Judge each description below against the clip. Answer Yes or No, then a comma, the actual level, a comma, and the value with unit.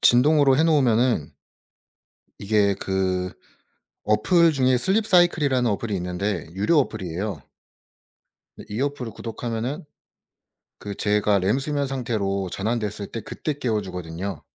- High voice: No, low, 110 Hz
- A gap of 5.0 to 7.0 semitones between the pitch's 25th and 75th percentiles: Yes, wide, 5.5 semitones